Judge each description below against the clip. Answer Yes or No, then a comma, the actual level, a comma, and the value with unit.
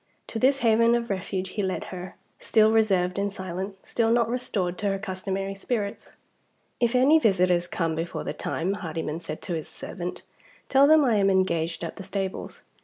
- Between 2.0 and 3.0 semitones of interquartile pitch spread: No, average, 3.8 semitones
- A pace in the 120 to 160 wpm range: No, average, 180 wpm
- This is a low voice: No, high, 195 Hz